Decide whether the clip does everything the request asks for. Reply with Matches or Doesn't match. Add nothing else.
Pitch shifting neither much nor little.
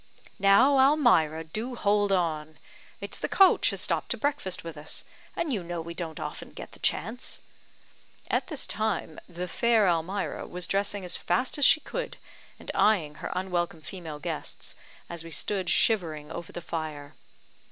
Matches